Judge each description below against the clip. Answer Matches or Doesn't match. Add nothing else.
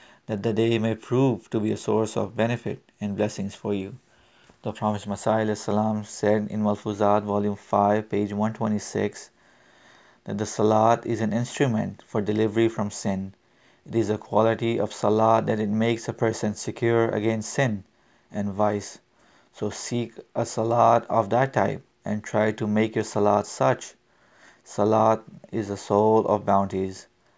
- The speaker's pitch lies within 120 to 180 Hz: Doesn't match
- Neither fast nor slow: Matches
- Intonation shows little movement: Matches